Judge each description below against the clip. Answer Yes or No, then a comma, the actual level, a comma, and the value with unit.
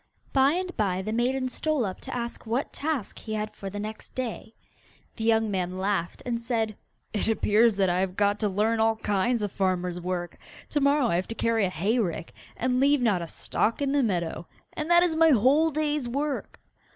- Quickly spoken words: Yes, fast, 210 wpm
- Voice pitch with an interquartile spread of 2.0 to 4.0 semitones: No, average, 5.3 semitones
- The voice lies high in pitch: Yes, high, 225 Hz